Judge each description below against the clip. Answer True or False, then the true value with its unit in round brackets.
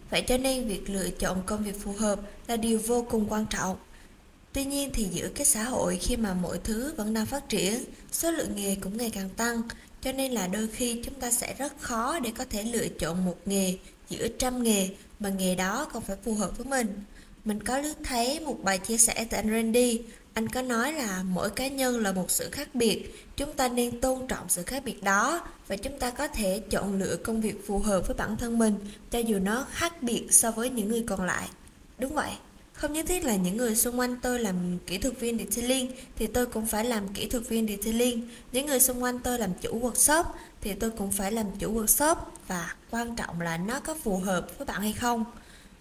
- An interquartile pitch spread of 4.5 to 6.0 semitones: False (3.8 semitones)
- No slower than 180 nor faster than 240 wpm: True (230 wpm)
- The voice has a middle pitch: False (225 Hz)